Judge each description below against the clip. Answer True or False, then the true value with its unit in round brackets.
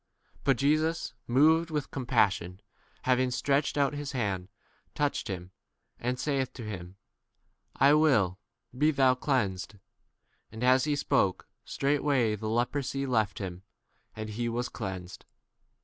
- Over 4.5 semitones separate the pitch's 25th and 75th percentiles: True (5.1 semitones)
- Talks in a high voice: False (125 Hz)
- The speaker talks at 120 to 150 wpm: True (145 wpm)